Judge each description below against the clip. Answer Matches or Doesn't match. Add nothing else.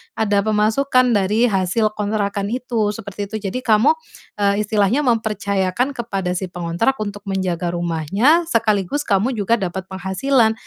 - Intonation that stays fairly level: Doesn't match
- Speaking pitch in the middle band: Doesn't match